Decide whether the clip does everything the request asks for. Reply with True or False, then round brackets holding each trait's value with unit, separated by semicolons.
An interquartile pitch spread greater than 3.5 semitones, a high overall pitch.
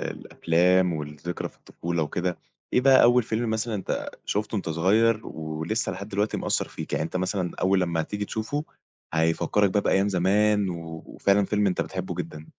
False (3.9 semitones; 95 Hz)